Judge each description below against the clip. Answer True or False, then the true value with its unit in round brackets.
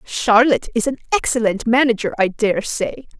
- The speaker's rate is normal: True (150 wpm)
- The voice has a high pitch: True (230 Hz)